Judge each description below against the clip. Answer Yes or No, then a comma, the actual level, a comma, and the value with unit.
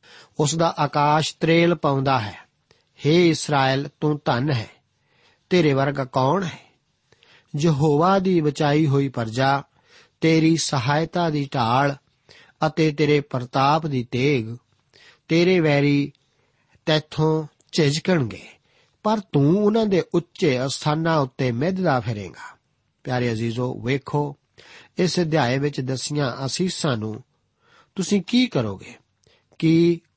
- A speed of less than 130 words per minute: Yes, average, 110 wpm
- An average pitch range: Yes, average, 3.5 semitones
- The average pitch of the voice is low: No, medium, 145 Hz